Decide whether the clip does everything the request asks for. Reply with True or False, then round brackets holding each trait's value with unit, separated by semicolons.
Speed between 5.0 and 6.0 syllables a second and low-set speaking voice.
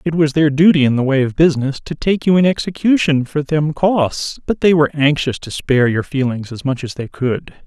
False (5.5 syllables/s; 150 Hz)